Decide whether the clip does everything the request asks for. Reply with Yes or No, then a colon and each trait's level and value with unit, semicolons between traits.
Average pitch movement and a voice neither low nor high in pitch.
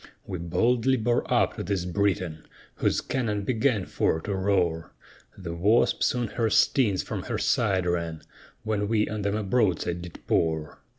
No: average, 4.1 semitones; low, 100 Hz